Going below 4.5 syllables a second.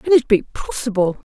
No: 5.0 syllables/s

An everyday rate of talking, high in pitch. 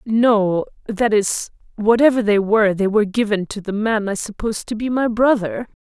Yes: average, 165 wpm; high, 215 Hz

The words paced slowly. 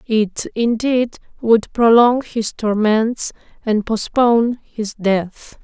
Yes: slow, 105 wpm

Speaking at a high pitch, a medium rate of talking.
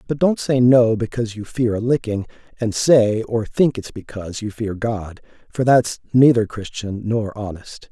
No: low, 115 Hz; average, 180 wpm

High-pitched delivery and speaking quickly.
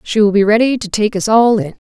Yes: high, 210 Hz; fast, 285 wpm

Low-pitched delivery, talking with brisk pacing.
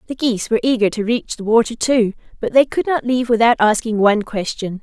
No: high, 230 Hz; fast, 225 wpm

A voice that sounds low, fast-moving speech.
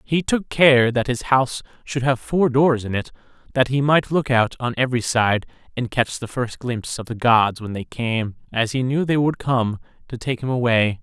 Yes: low, 125 Hz; fast, 225 wpm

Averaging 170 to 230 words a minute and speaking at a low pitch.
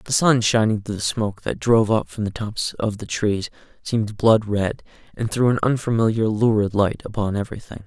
Yes: average, 200 wpm; low, 110 Hz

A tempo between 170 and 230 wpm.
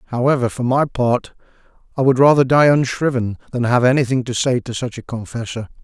Yes: average, 185 wpm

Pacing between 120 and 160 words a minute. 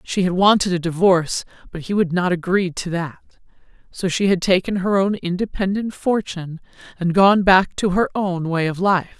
No: average, 190 wpm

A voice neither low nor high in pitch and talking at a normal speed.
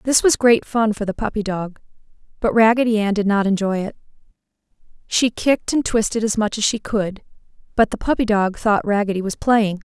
No: high, 215 Hz; average, 195 wpm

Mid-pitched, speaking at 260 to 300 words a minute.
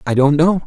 Yes: medium, 155 Hz; fast, 270 wpm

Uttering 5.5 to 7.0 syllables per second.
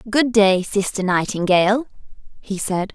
No: 4.5 syllables/s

